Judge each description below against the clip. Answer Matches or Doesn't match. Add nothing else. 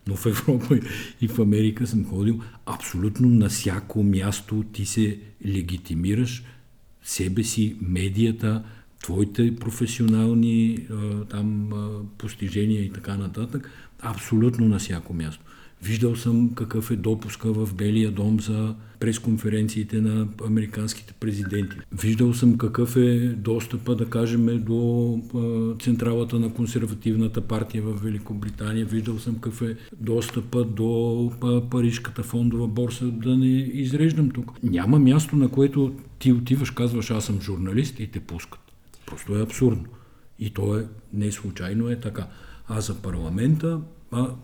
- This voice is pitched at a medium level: Doesn't match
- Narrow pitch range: Matches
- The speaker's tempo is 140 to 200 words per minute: Doesn't match